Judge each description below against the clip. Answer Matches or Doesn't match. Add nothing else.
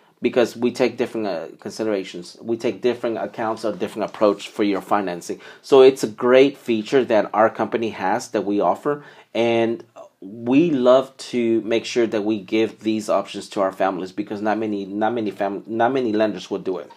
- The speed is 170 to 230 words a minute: Matches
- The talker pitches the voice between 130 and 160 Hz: Doesn't match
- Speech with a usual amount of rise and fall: Doesn't match